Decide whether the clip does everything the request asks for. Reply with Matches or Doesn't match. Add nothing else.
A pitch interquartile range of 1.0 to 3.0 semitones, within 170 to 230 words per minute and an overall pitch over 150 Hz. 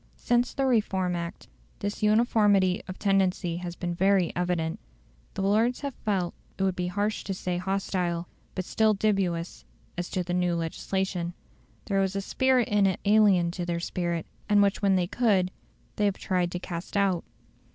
Matches